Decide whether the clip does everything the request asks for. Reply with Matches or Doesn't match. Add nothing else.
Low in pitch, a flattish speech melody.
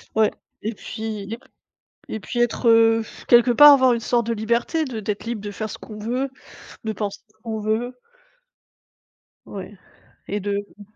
Doesn't match